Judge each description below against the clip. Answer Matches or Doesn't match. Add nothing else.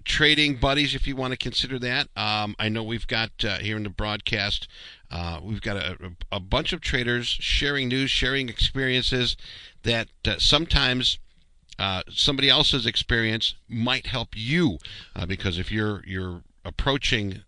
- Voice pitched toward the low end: Matches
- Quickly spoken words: Doesn't match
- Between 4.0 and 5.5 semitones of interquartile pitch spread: Matches